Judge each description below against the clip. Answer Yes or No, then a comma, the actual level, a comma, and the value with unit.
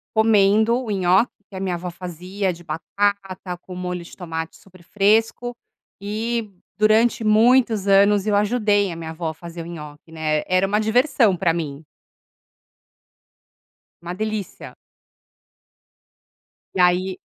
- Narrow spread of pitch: No, average, 3.5 semitones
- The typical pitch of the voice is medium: No, high, 195 Hz